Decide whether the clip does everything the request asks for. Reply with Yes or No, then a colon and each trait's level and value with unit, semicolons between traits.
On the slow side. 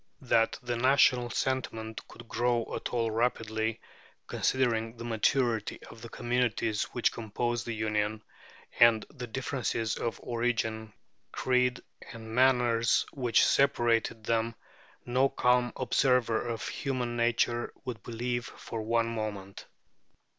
Yes: slow, 120 wpm